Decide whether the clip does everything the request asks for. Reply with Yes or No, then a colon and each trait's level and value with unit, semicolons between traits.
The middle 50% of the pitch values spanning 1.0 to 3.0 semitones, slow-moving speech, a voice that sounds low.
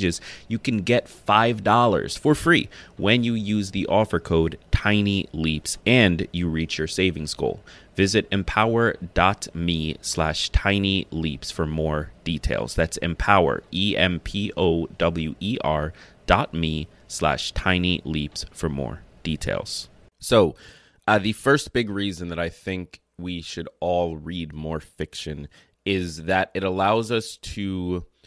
No: average, 3.9 semitones; slow, 125 wpm; very low, 90 Hz